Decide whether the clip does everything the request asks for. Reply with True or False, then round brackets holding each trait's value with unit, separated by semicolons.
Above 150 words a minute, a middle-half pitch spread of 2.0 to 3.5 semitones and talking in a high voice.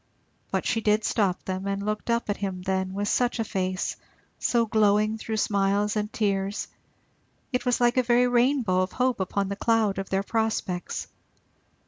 True (175 wpm; 2.8 semitones; 210 Hz)